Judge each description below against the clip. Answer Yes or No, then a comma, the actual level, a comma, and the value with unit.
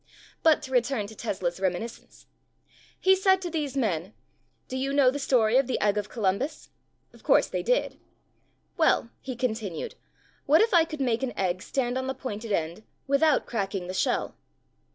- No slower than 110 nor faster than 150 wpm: No, average, 175 wpm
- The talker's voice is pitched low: No, very high, 250 Hz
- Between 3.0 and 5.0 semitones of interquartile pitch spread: No, wide, 5.4 semitones